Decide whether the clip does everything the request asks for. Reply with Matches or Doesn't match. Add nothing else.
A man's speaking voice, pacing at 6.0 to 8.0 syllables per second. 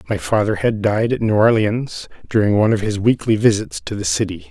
Doesn't match